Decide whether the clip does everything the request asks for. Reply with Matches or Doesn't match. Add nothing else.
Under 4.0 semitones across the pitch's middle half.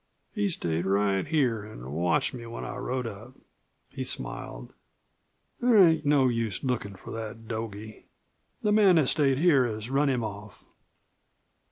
Doesn't match